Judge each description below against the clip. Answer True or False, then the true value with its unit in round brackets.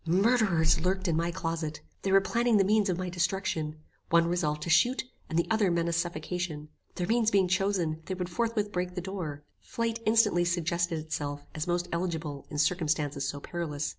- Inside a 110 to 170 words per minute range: False (185 wpm)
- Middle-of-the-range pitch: True (175 Hz)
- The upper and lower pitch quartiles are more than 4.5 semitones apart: False (3.3 semitones)